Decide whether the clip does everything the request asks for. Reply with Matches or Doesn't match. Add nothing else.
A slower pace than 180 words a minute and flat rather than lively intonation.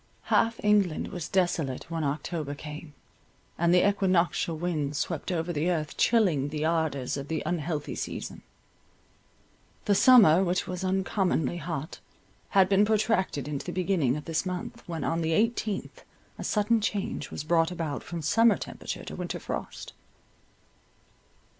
Doesn't match